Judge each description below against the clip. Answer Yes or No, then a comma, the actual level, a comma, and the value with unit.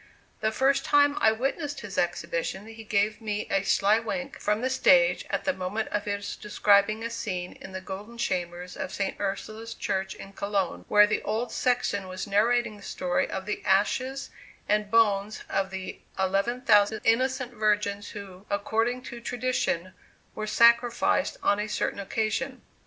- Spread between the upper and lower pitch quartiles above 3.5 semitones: No, average, 3.1 semitones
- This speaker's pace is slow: No, average, 165 wpm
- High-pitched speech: Yes, high, 210 Hz